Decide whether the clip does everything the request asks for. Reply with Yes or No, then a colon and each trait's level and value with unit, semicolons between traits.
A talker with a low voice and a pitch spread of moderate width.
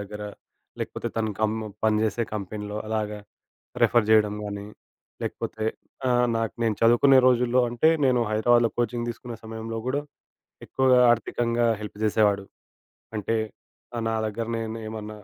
No: low, 115 Hz; narrow, 2.0 semitones